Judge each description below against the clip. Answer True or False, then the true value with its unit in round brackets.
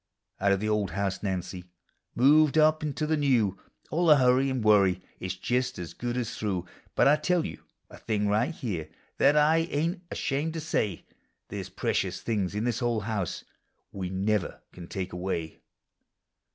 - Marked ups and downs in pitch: True (7.1 semitones)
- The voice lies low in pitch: True (110 Hz)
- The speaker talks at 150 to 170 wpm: False (180 wpm)